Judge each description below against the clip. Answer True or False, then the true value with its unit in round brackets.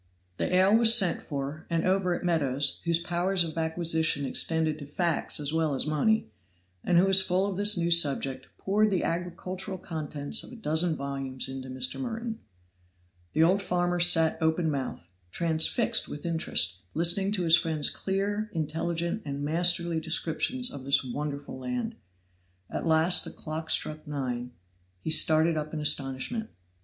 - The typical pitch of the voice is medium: True (165 Hz)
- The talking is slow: False (160 wpm)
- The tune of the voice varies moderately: True (3.6 semitones)